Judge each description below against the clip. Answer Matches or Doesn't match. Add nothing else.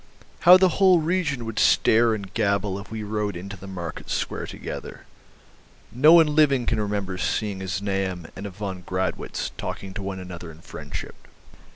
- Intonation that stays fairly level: Doesn't match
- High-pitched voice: Doesn't match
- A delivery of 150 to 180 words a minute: Matches